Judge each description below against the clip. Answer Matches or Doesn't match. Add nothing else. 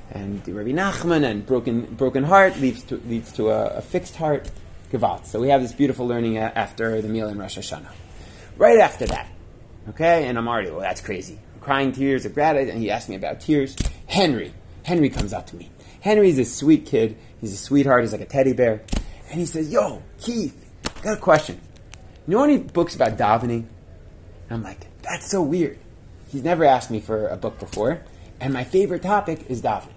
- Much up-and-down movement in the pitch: Matches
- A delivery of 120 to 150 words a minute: Doesn't match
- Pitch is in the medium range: Doesn't match